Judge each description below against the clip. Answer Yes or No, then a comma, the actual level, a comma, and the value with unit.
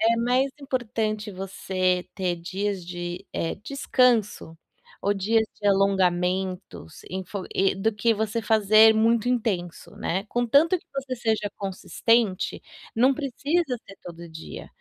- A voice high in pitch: Yes, high, 210 Hz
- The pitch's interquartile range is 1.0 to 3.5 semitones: No, average, 4.0 semitones